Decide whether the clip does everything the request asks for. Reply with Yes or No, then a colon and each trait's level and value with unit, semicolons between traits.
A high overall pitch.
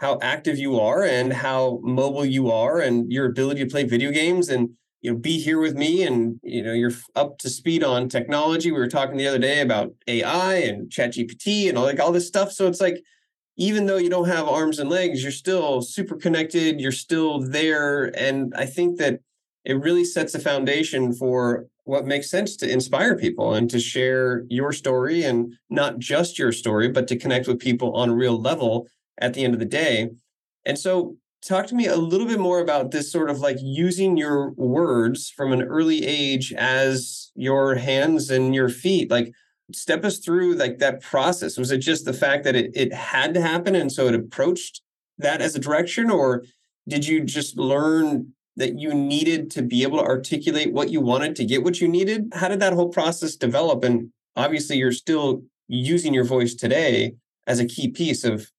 No: medium, 140 Hz